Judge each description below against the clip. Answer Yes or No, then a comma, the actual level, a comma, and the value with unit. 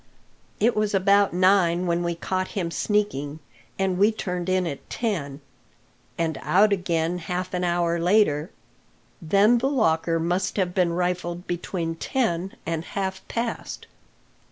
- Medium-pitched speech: Yes, medium, 180 Hz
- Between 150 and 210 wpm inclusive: No, slow, 135 wpm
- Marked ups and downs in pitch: No, average, 2.8 semitones